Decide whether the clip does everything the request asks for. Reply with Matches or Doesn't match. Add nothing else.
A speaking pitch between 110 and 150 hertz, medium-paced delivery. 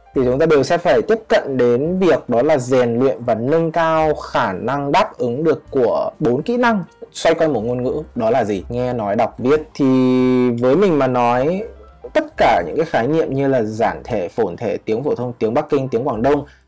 Matches